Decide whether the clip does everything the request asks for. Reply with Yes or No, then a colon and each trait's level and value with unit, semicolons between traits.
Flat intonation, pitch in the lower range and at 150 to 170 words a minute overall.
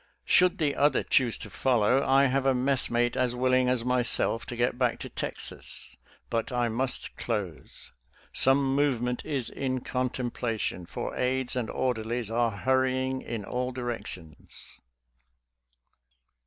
No: narrow, 1.8 semitones; low, 125 Hz; slow, 135 wpm